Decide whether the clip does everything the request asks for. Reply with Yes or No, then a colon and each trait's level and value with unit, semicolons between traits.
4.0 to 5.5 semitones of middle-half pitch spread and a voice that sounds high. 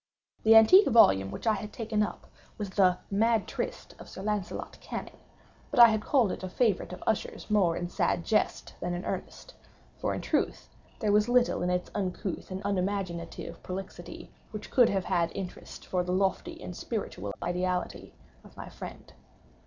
No: average, 3.3 semitones; high, 195 Hz